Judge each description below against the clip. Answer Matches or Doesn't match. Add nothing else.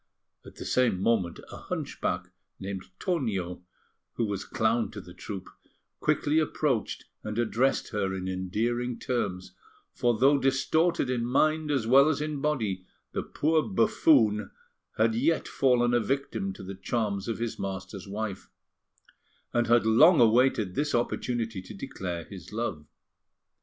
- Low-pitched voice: Matches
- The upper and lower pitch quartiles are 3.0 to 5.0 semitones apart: Doesn't match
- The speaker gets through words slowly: Doesn't match